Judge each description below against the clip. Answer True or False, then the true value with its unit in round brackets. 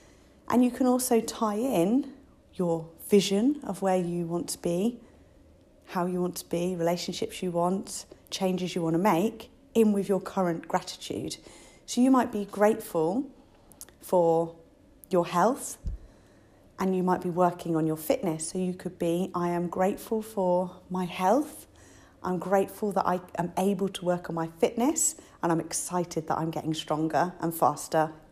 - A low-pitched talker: False (180 Hz)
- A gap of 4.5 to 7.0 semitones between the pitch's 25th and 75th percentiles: False (3.8 semitones)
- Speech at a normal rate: True (165 wpm)